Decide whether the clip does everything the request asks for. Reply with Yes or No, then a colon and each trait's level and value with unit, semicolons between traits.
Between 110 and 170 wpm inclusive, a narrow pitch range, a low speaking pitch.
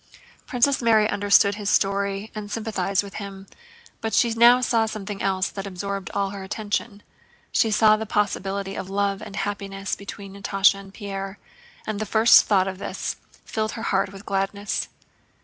No: average, 165 wpm; narrow, 1.6 semitones; high, 200 Hz